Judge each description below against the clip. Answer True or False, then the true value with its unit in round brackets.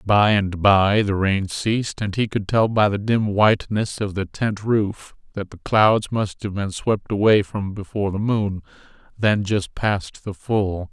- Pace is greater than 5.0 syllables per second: False (4.1 syllables/s)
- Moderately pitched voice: False (105 Hz)